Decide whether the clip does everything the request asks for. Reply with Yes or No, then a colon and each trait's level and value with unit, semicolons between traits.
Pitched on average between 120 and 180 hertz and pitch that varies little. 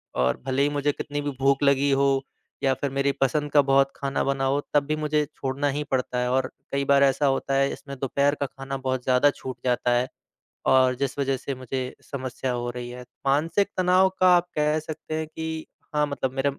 Yes: medium, 140 Hz; narrow, 1.8 semitones